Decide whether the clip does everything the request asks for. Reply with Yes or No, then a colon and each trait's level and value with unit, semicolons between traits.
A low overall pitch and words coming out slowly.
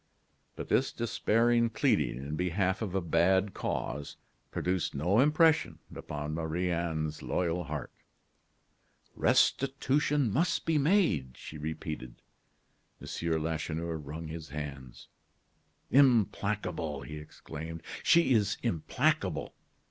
Yes: very low, 85 Hz; slow, 105 wpm